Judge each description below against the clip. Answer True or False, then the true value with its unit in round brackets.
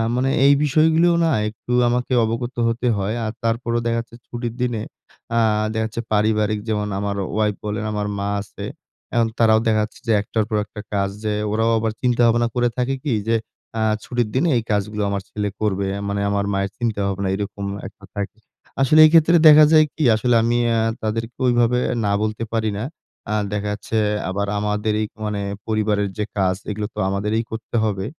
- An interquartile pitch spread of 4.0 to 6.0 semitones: False (2.4 semitones)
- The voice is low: True (110 Hz)